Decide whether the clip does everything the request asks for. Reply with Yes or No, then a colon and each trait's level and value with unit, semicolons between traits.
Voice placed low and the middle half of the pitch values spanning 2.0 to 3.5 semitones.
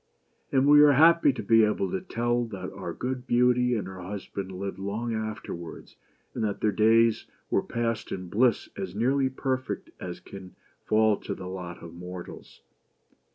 No: low, 110 Hz; average, 4.6 semitones